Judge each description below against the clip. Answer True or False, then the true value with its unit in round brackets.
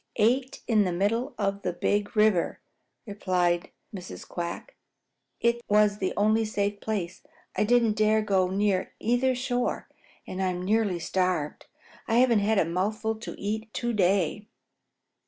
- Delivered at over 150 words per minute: False (145 wpm)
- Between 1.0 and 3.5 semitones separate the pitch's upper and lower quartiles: True (3.1 semitones)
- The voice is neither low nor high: False (210 Hz)